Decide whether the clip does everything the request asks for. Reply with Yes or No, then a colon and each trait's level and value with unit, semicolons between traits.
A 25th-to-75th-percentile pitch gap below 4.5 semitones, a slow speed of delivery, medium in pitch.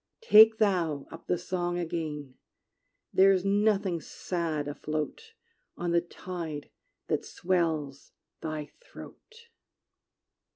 Yes: average, 3.6 semitones; slow, 100 wpm; medium, 175 Hz